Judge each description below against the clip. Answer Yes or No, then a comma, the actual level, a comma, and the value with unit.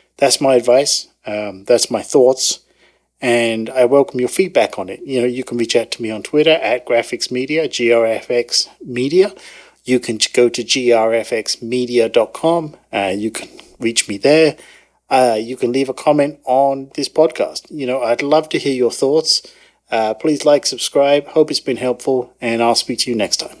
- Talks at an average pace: Yes, average, 185 wpm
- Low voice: Yes, low, 125 Hz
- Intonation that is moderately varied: Yes, average, 4.2 semitones